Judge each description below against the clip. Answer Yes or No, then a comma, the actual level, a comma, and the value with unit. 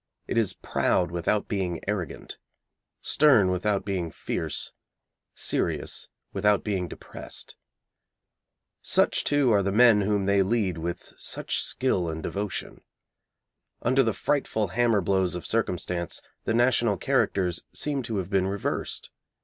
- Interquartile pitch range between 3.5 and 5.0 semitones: Yes, average, 3.9 semitones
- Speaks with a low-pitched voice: Yes, low, 100 Hz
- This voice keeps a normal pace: No, slow, 130 wpm